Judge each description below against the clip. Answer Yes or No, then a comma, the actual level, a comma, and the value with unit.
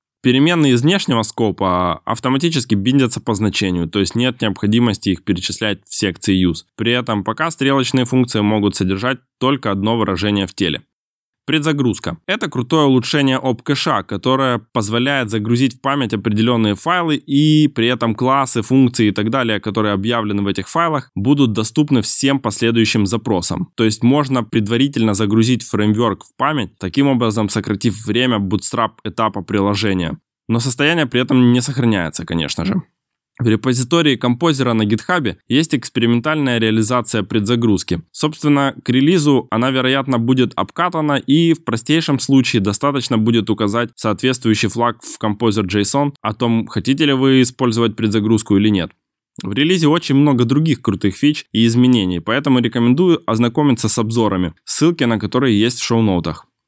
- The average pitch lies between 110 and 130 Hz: Yes, low, 120 Hz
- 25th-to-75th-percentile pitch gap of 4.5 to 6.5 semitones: No, average, 3.8 semitones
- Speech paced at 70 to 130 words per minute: No, average, 150 wpm